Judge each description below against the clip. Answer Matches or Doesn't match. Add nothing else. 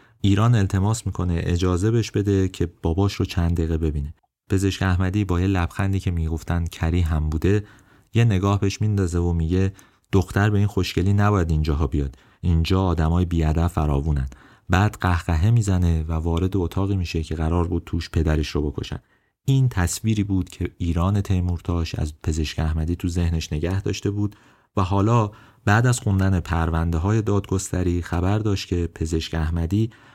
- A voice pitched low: Matches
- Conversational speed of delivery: Doesn't match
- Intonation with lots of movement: Doesn't match